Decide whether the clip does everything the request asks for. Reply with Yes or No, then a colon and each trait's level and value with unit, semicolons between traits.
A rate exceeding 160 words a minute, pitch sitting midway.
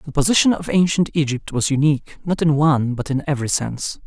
Yes: fast, 205 wpm; medium, 150 Hz